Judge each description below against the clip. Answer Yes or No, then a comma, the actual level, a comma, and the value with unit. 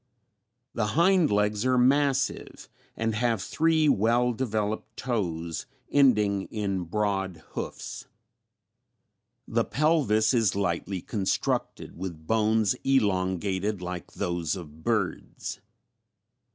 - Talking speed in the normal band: No, slow, 100 wpm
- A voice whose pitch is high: No, low, 105 Hz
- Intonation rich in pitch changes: No, average, 4.7 semitones